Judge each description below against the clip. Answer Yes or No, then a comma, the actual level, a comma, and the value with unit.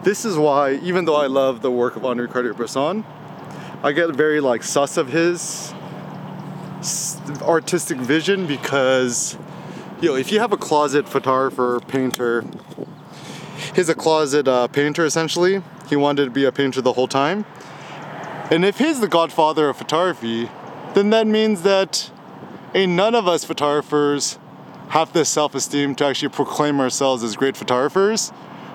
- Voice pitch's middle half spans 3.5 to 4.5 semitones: Yes, average, 4.2 semitones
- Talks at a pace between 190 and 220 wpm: No, average, 150 wpm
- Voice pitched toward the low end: No, medium, 150 Hz